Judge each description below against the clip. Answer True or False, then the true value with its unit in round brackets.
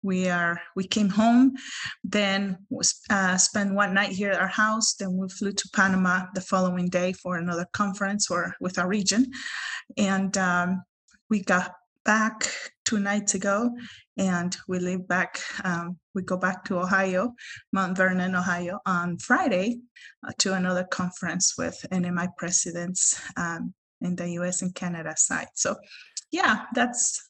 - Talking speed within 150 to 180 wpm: True (155 wpm)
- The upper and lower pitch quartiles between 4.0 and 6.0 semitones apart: False (2.7 semitones)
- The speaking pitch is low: False (190 Hz)